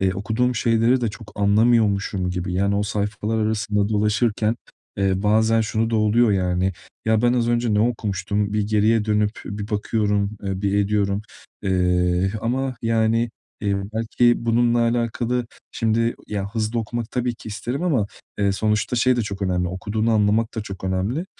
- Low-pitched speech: Yes, low, 105 Hz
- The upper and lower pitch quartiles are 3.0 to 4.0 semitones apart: No, narrow, 2.4 semitones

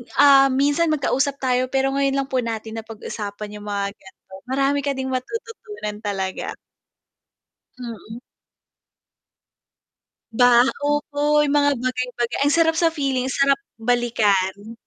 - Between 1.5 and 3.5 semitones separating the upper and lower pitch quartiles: No, average, 4.3 semitones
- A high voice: Yes, very high, 255 Hz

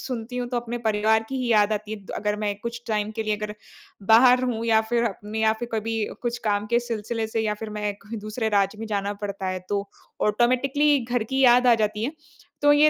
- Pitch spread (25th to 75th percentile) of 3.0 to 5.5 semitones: No, narrow, 2.4 semitones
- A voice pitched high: Yes, high, 220 Hz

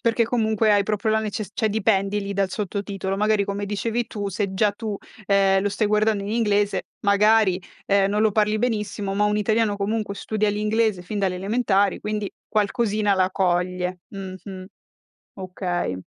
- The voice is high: Yes, high, 205 Hz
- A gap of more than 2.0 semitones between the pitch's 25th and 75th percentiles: No, narrow, 1.7 semitones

